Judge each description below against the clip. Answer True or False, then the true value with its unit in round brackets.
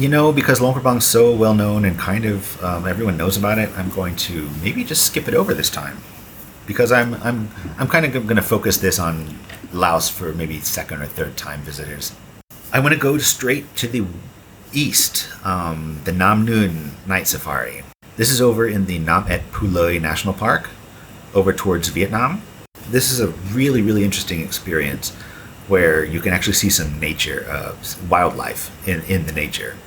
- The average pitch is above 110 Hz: False (100 Hz)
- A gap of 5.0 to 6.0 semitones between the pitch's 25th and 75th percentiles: True (5.4 semitones)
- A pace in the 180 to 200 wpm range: True (185 wpm)